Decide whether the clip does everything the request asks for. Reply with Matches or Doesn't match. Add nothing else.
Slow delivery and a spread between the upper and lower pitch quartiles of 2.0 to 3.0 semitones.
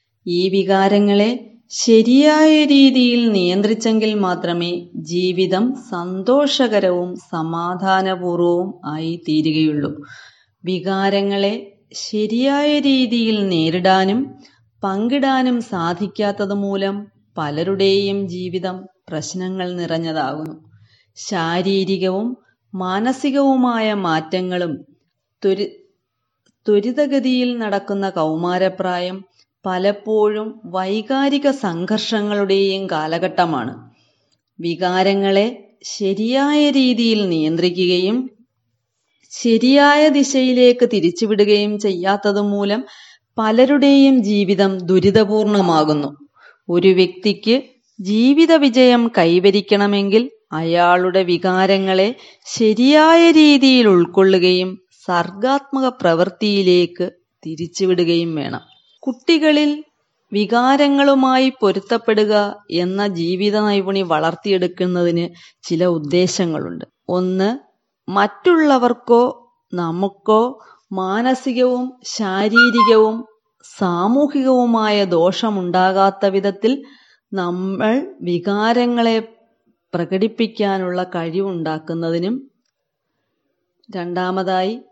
Doesn't match